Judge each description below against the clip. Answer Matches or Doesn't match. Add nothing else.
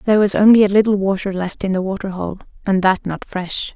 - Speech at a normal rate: Doesn't match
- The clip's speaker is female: Matches